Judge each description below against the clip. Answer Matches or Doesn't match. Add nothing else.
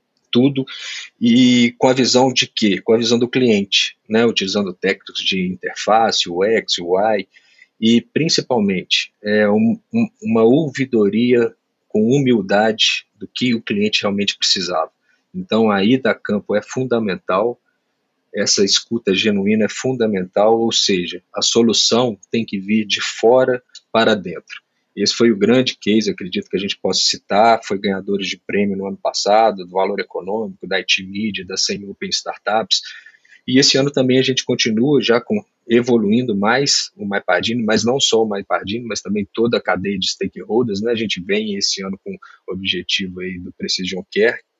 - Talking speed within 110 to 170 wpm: Matches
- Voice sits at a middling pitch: Doesn't match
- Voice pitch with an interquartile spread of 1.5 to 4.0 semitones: Doesn't match